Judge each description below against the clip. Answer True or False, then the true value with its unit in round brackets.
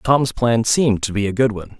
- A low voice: True (115 Hz)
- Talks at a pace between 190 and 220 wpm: False (270 wpm)